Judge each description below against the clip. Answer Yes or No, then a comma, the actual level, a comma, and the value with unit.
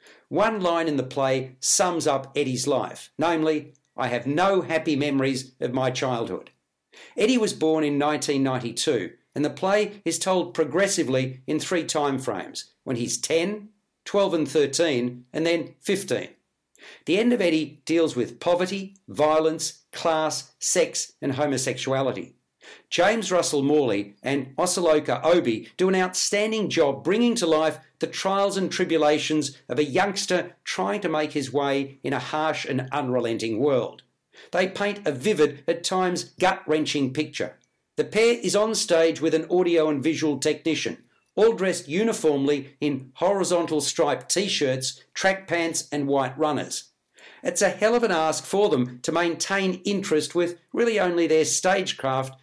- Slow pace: No, average, 150 wpm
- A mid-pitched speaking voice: Yes, medium, 155 Hz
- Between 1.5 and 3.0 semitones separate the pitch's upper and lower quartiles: No, average, 4.3 semitones